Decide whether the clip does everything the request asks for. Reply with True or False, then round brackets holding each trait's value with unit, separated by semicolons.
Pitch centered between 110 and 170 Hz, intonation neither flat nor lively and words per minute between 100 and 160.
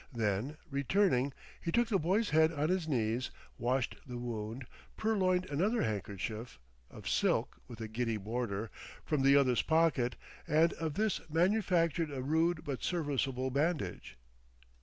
False (140 Hz; 5.8 semitones; 140 wpm)